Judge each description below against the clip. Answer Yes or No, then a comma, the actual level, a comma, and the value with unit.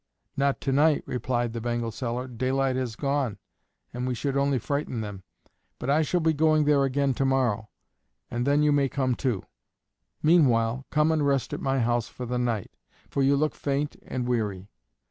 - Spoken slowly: No, average, 185 wpm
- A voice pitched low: Yes, low, 130 Hz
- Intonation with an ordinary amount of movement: Yes, average, 3.0 semitones